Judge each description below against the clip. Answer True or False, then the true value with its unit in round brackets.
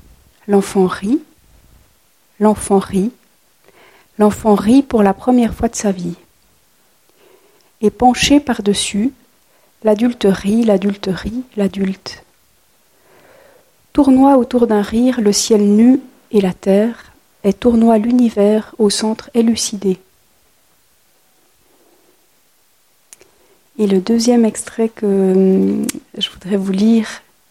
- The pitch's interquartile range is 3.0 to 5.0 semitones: True (3.7 semitones)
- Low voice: False (220 Hz)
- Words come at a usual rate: False (100 wpm)